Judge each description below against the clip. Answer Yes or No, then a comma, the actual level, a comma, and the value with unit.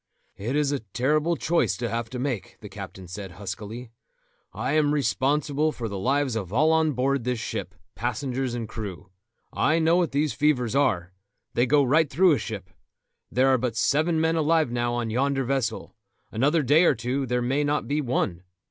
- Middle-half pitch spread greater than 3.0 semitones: Yes, average, 4.4 semitones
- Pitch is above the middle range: No, low, 130 Hz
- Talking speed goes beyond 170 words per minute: Yes, average, 190 wpm